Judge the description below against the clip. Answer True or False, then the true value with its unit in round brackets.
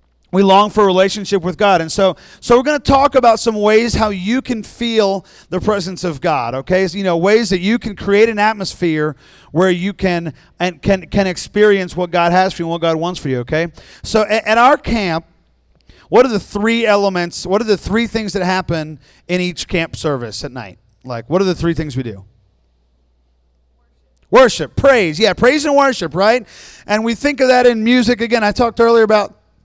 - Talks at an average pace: False (215 wpm)